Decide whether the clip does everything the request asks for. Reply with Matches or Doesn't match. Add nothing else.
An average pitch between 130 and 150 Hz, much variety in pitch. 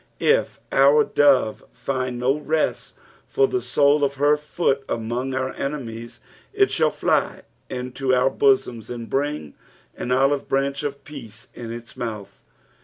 Doesn't match